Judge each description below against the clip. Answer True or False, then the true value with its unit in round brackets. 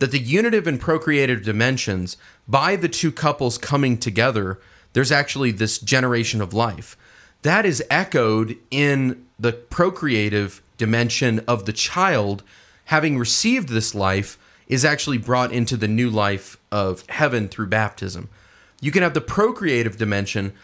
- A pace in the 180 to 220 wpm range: False (140 wpm)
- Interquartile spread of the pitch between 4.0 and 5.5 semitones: True (5.1 semitones)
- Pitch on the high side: False (120 Hz)